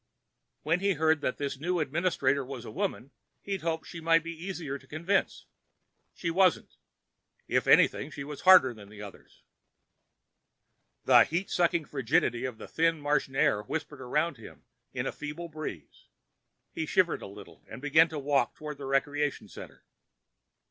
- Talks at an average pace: Yes, average, 160 wpm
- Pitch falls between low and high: Yes, medium, 150 Hz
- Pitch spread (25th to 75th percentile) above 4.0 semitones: No, average, 3.5 semitones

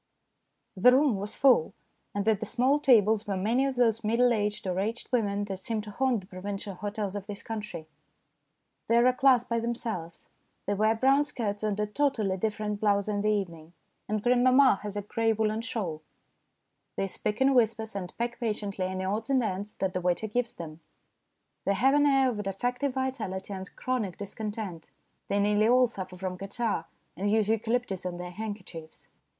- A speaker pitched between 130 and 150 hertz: No, high, 210 Hz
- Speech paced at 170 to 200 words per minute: Yes, average, 185 wpm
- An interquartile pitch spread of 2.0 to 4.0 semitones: Yes, average, 3.4 semitones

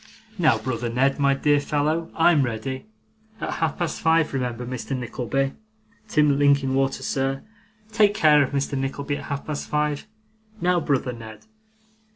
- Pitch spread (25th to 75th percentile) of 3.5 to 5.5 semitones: No, narrow, 2.4 semitones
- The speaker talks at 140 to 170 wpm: Yes, average, 150 wpm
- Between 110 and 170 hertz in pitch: Yes, medium, 140 Hz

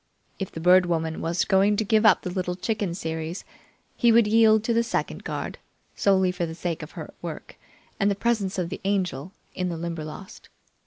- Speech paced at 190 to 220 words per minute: Yes, average, 200 wpm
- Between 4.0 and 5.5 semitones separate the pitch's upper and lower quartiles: No, average, 3.6 semitones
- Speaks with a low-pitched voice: No, medium, 185 Hz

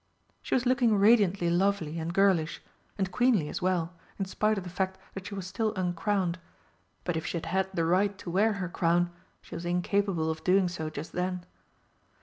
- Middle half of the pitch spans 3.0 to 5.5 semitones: No, narrow, 2.6 semitones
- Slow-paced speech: No, average, 195 wpm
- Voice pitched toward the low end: No, medium, 185 Hz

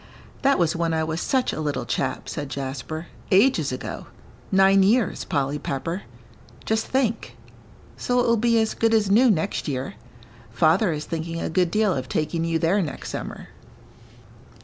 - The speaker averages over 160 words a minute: Yes, average, 170 wpm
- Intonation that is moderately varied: No, wide, 5.9 semitones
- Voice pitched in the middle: Yes, medium, 170 Hz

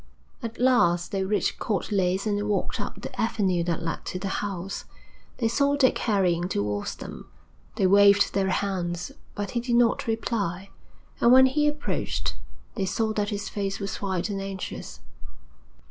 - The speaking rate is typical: Yes, average, 165 wpm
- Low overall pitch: No, high, 200 Hz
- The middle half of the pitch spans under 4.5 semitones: Yes, average, 3.3 semitones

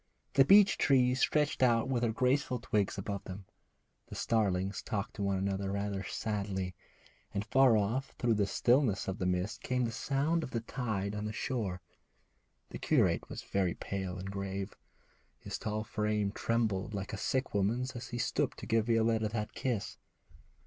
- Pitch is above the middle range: No, low, 110 Hz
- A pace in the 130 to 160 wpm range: No, average, 170 wpm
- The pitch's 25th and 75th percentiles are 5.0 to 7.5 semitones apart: No, average, 3.9 semitones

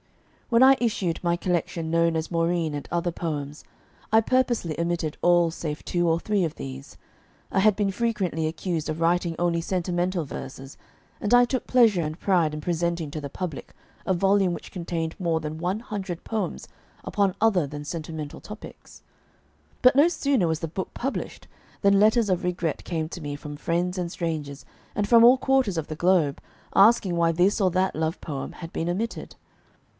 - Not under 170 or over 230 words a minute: Yes, average, 180 wpm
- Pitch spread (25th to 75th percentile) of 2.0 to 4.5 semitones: Yes, average, 3.6 semitones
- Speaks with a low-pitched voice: No, medium, 175 Hz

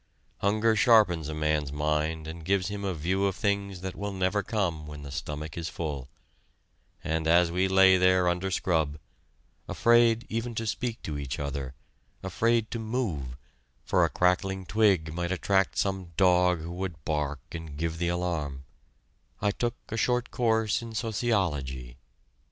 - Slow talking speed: No, average, 160 wpm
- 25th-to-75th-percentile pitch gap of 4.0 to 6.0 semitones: Yes, average, 4.7 semitones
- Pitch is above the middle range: No, very low, 90 Hz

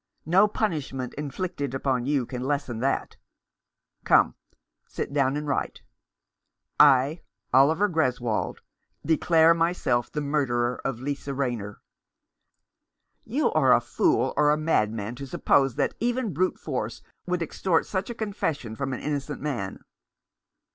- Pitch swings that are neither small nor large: Yes, average, 4.1 semitones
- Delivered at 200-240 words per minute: No, slow, 135 wpm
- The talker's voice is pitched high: No, medium, 140 Hz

